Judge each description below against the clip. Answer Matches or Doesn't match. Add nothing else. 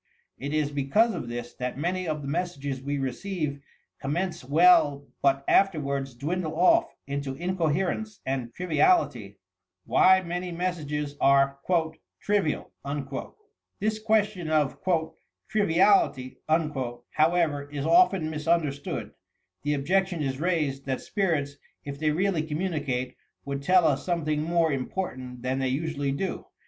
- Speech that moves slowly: Matches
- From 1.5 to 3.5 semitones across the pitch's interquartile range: Doesn't match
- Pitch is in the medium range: Matches